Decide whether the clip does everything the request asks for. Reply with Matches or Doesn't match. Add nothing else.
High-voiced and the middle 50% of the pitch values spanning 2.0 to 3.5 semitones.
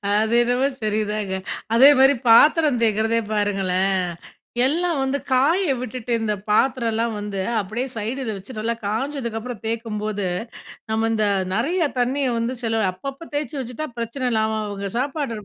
Doesn't match